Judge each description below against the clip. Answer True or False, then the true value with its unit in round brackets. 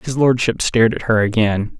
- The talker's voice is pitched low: True (110 Hz)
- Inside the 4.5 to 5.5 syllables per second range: True (5.3 syllables/s)